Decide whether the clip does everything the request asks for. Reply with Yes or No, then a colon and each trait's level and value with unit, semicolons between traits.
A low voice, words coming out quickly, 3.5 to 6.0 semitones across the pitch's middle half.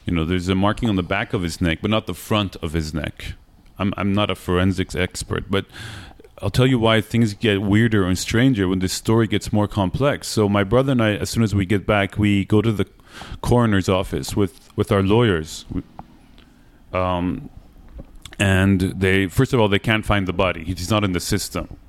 No: low, 100 Hz; fast, 210 wpm; average, 2.7 semitones